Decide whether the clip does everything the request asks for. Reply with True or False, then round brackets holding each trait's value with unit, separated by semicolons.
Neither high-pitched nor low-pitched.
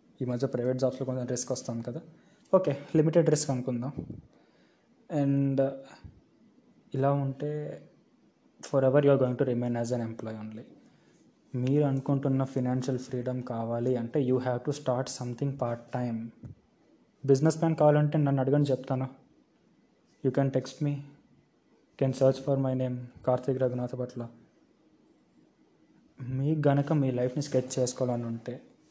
False (130 Hz)